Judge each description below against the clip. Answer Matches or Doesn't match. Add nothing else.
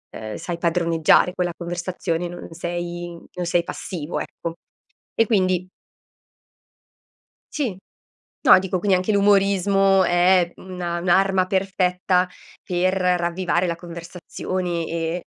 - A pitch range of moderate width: Doesn't match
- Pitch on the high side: Doesn't match